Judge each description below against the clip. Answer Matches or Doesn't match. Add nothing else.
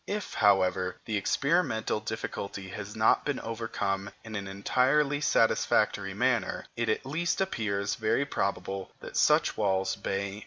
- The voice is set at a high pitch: Doesn't match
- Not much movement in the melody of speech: Doesn't match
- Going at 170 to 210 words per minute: Doesn't match